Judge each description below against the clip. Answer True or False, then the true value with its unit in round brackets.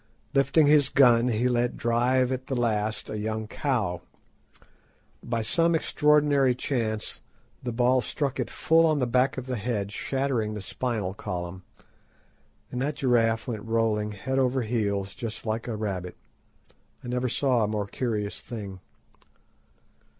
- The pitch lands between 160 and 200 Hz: False (120 Hz)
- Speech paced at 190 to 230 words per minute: False (150 wpm)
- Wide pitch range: False (3.4 semitones)